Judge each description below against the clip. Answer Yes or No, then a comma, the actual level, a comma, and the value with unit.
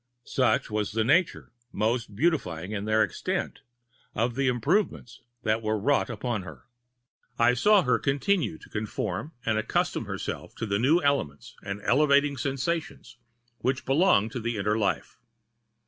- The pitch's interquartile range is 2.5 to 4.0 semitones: No, average, 4.6 semitones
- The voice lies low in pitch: Yes, low, 120 Hz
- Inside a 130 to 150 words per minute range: Yes, average, 140 wpm